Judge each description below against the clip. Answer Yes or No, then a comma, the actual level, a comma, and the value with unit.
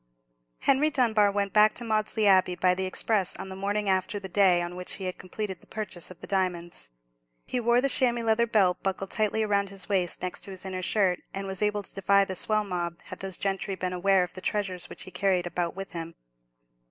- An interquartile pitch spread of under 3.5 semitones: Yes, narrow, 2.4 semitones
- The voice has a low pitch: No, high, 195 Hz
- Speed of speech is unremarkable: No, fast, 225 wpm